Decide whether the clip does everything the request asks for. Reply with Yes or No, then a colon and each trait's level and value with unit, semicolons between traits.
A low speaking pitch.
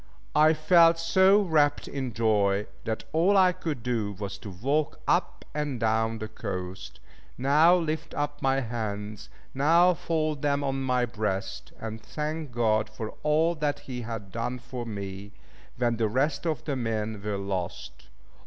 Yes: low, 125 Hz